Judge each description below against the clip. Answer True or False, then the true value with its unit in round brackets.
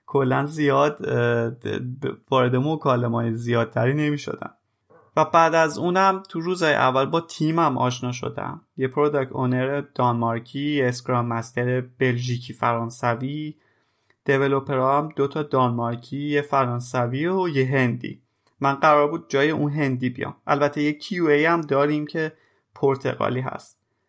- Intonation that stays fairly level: False (3.2 semitones)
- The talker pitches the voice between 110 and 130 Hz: False (140 Hz)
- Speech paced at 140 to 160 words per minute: False (130 wpm)